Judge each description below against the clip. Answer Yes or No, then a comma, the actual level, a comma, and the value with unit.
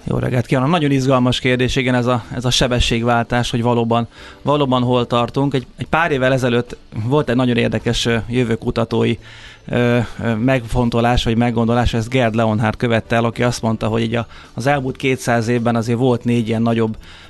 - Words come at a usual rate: No, fast, 180 wpm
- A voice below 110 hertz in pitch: No, low, 120 Hz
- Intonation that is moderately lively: No, narrow, 1.7 semitones